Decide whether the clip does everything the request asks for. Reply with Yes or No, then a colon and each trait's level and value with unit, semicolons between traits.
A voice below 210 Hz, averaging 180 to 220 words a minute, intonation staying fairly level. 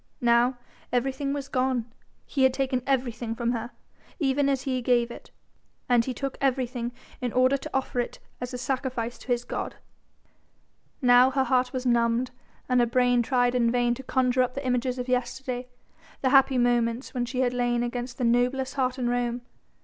No: very high, 250 Hz; average, 185 wpm; narrow, 1.4 semitones